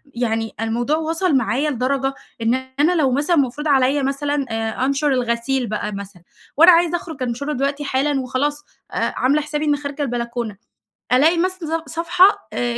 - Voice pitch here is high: Yes, very high, 275 Hz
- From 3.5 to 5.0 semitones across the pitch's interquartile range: Yes, average, 3.8 semitones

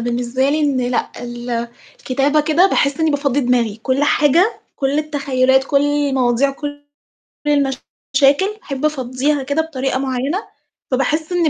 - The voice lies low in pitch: No, very high, 275 Hz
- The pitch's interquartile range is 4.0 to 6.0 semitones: No, average, 2.7 semitones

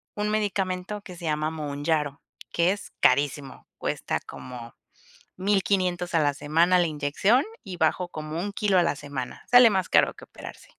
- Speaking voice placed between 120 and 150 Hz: No, medium, 175 Hz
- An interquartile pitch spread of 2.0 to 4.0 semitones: No, average, 4.6 semitones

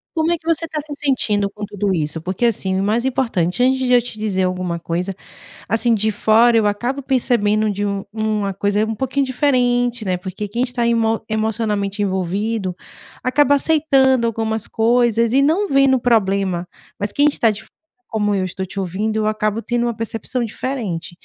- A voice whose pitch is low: No, high, 220 Hz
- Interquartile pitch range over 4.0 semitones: No, average, 3.7 semitones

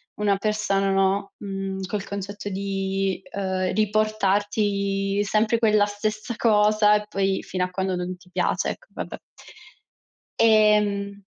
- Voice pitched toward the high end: Yes, high, 200 Hz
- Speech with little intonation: Yes, narrow, 1.5 semitones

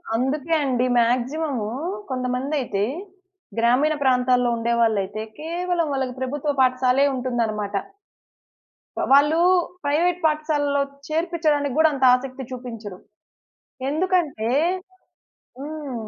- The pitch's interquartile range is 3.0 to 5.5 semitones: Yes, average, 3.7 semitones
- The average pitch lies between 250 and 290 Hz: Yes, very high, 265 Hz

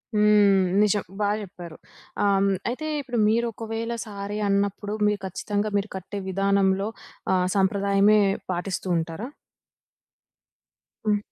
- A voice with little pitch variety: Yes, narrow, 1.6 semitones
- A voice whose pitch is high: Yes, high, 200 Hz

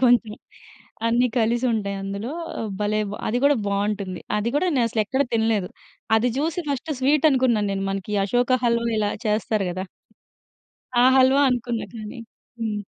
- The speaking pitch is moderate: No, high, 225 Hz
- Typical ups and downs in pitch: Yes, average, 3.3 semitones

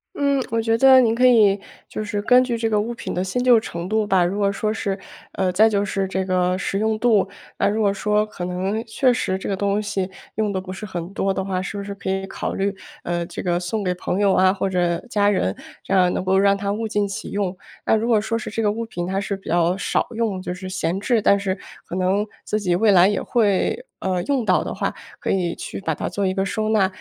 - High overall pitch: Yes, high, 200 Hz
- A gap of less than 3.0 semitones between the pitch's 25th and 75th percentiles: Yes, narrow, 2.6 semitones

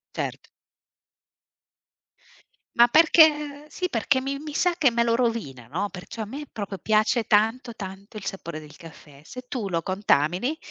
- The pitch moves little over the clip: No, wide, 6.3 semitones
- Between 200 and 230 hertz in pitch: Yes, high, 225 Hz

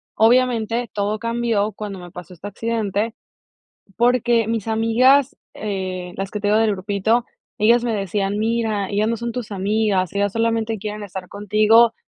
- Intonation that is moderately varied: No, narrow, 2.3 semitones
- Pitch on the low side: No, high, 215 Hz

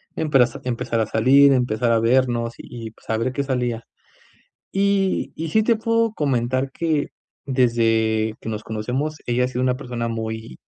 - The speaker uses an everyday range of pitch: Yes, average, 3.6 semitones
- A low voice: Yes, low, 125 Hz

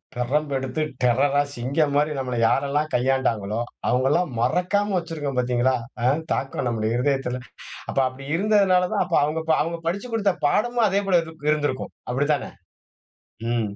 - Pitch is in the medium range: Yes, medium, 145 Hz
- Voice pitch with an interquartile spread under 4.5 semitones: No, average, 5.3 semitones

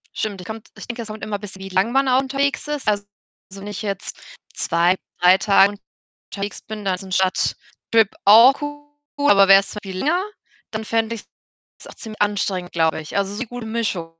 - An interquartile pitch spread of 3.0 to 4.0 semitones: Yes, average, 3.4 semitones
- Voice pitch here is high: Yes, high, 210 Hz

